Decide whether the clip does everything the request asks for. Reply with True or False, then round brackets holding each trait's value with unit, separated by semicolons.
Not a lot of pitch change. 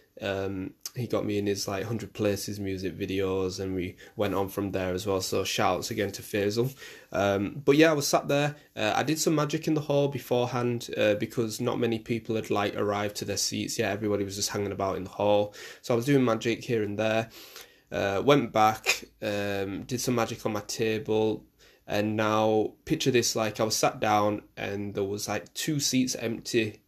False (3.3 semitones)